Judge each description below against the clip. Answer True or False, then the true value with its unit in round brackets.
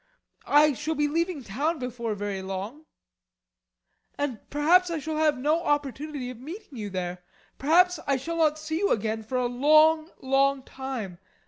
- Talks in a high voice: True (285 Hz)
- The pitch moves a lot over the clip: False (4.4 semitones)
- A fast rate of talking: False (160 wpm)